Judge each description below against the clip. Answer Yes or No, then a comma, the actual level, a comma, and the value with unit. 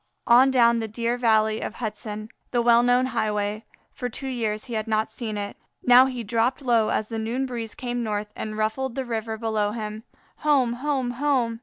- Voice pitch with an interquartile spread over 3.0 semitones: No, narrow, 2.4 semitones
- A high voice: Yes, high, 230 Hz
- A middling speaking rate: Yes, average, 195 wpm